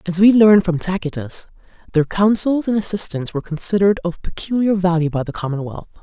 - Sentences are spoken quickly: No, average, 170 wpm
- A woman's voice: Yes, female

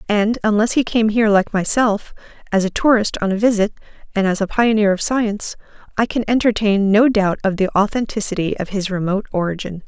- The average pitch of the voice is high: Yes, high, 210 Hz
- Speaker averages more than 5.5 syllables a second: Yes, 5.8 syllables/s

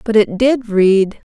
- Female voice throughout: Yes, female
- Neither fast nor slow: Yes, average, 180 wpm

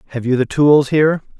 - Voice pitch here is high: No, medium, 140 Hz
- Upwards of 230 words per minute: No, fast, 215 wpm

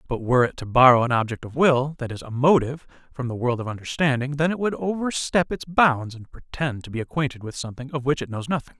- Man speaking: Yes, male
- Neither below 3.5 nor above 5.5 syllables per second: No, 6.2 syllables/s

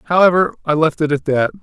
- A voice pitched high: No, medium, 160 Hz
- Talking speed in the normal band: No, fast, 220 wpm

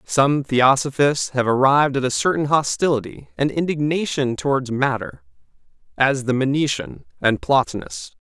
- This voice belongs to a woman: No, male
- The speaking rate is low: Yes, slow, 125 wpm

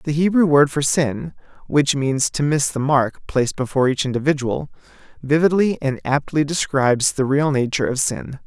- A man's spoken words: Yes, male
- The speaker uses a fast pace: No, average, 170 wpm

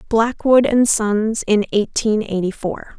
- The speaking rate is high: No, average, 140 wpm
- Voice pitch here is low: No, high, 215 Hz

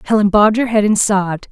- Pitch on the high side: Yes, high, 205 Hz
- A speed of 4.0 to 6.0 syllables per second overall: No, 6.5 syllables/s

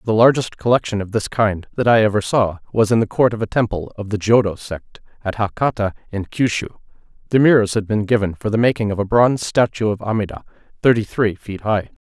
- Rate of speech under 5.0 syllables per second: No, 5.9 syllables/s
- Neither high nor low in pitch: No, low, 110 Hz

